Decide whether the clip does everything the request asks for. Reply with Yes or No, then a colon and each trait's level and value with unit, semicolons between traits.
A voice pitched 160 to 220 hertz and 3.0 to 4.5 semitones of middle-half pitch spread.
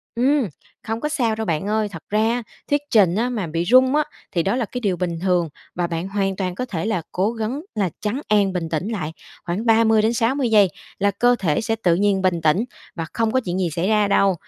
Yes: high, 205 Hz; average, 4.1 semitones